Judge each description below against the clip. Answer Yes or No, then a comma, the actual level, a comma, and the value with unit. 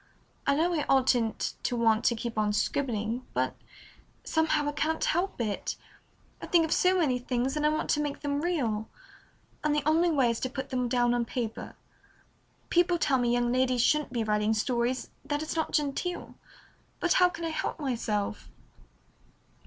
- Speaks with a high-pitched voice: Yes, very high, 265 Hz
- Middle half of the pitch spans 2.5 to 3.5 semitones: No, average, 4.6 semitones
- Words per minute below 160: No, average, 180 wpm